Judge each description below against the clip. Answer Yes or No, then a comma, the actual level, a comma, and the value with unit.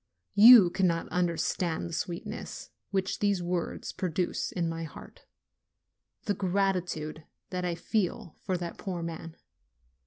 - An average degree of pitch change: No, narrow, 2.3 semitones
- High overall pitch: No, medium, 180 Hz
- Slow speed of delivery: Yes, slow, 125 wpm